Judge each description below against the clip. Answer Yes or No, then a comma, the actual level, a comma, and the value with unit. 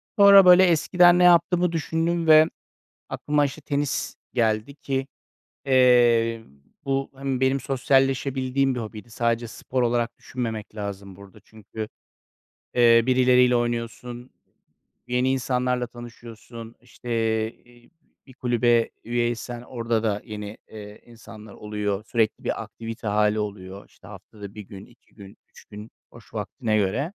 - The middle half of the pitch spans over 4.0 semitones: No, average, 3.5 semitones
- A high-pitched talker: No, low, 120 Hz